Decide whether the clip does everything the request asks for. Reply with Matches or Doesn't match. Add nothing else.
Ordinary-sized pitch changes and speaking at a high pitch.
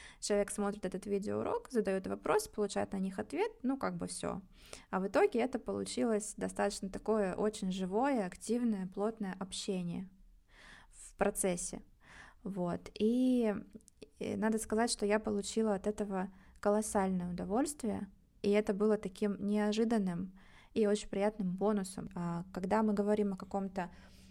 Doesn't match